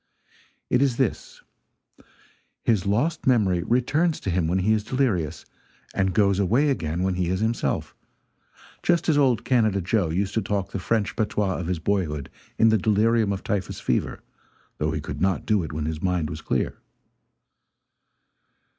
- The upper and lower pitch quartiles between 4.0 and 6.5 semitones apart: Yes, average, 4.3 semitones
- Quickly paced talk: No, average, 165 wpm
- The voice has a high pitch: No, low, 100 Hz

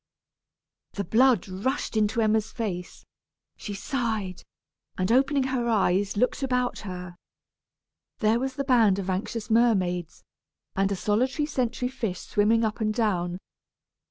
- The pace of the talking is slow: Yes, slow, 130 wpm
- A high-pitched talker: Yes, high, 220 Hz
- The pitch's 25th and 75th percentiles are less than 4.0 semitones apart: No, average, 4.3 semitones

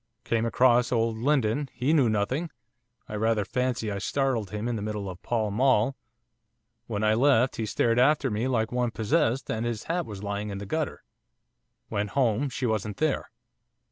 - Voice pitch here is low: Yes, low, 115 Hz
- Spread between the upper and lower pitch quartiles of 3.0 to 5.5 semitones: Yes, average, 3.5 semitones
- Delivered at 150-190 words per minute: Yes, average, 180 wpm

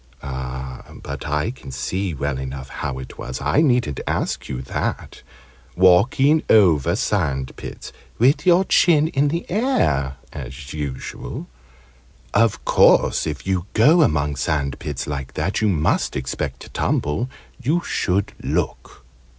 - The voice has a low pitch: Yes, very low, 75 Hz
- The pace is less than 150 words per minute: Yes, slow, 135 wpm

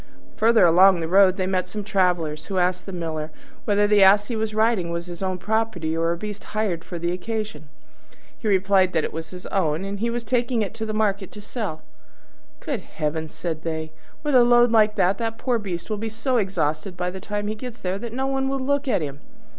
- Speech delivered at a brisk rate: Yes, fast, 230 wpm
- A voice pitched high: Yes, high, 195 Hz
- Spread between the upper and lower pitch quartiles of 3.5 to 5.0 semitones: Yes, average, 4.2 semitones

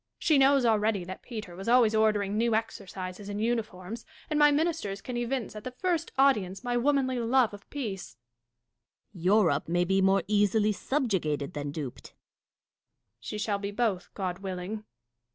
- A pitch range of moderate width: Yes, average, 4.1 semitones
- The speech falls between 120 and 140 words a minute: No, average, 165 wpm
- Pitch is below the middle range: No, high, 210 Hz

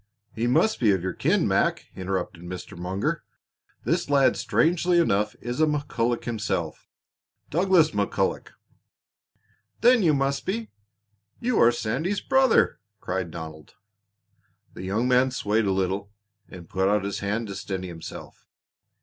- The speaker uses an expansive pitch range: Yes, wide, 7.9 semitones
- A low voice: Yes, low, 110 Hz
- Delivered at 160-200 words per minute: No, average, 140 wpm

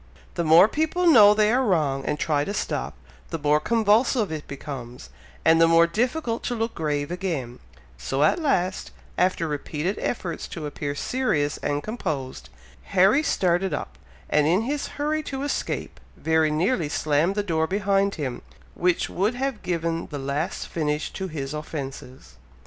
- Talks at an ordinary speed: Yes, average, 160 wpm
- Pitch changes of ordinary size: No, wide, 6.1 semitones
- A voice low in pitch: No, medium, 170 Hz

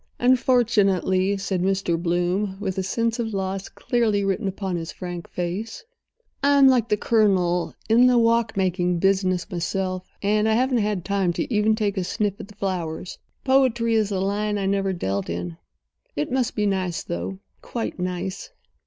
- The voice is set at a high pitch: Yes, high, 195 Hz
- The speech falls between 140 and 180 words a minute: Yes, average, 160 wpm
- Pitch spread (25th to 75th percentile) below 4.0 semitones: Yes, average, 3.3 semitones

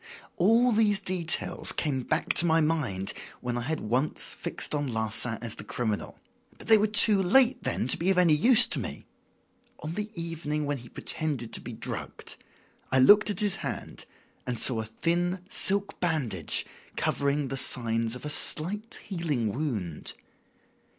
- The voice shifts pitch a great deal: Yes, wide, 7.5 semitones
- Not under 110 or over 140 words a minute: No, average, 170 wpm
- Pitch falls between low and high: Yes, medium, 150 Hz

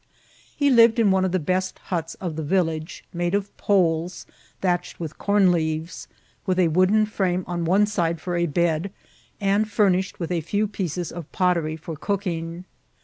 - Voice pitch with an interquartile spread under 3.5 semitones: Yes, average, 2.9 semitones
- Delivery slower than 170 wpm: No, average, 175 wpm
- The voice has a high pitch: No, medium, 180 Hz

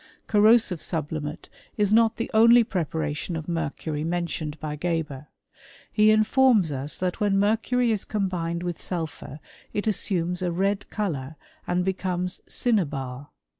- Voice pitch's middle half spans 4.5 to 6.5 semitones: Yes, average, 5.0 semitones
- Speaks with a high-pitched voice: No, medium, 180 Hz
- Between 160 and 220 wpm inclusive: No, slow, 135 wpm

